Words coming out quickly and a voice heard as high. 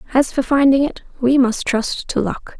Yes: fast, 210 wpm; very high, 260 Hz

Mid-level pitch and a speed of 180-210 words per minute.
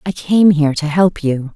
No: medium, 165 Hz; fast, 230 wpm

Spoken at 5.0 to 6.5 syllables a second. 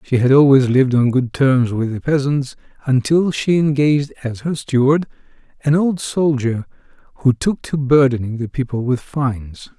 No: 4.8 syllables/s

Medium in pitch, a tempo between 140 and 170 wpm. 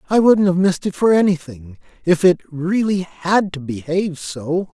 Yes: medium, 175 Hz; average, 165 wpm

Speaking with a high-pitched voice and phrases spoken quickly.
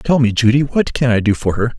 No: low, 120 Hz; fast, 300 wpm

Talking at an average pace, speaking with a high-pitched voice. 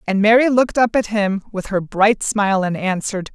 No: fast, 215 wpm; high, 205 Hz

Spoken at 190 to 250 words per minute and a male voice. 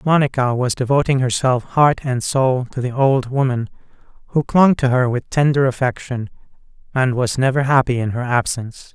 No: average, 170 wpm; male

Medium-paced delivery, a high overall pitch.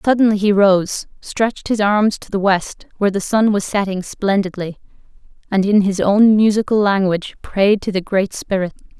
Yes: average, 175 wpm; high, 200 Hz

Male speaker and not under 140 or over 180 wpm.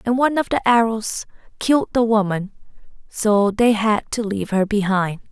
No: female; average, 170 wpm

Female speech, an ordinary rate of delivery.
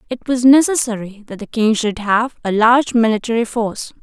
Yes: female; average, 180 wpm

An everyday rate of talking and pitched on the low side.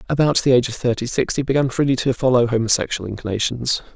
Yes: average, 195 wpm; low, 125 Hz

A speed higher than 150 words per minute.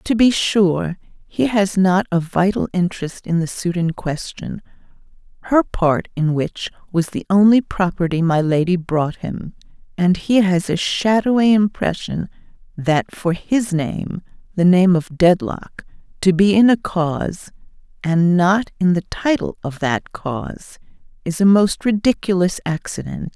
No: average, 145 wpm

